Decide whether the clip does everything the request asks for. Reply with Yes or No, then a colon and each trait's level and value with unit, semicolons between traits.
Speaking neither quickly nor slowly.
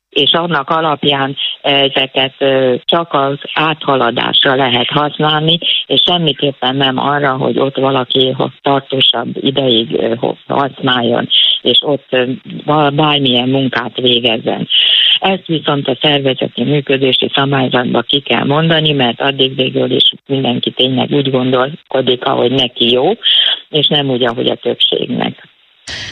Yes: average, 115 wpm